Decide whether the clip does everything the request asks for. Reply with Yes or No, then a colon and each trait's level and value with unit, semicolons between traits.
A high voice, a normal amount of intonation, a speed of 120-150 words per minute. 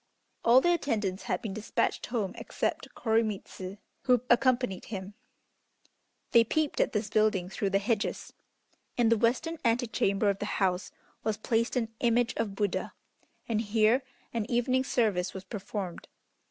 Yes: high, 220 Hz; average, 3.2 semitones; average, 145 wpm